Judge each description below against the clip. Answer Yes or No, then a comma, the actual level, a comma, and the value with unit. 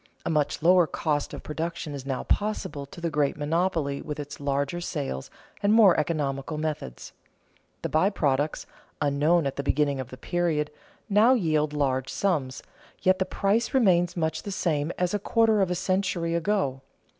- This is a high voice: No, medium, 160 Hz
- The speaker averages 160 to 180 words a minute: Yes, average, 170 wpm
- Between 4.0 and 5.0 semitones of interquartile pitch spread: Yes, average, 4.4 semitones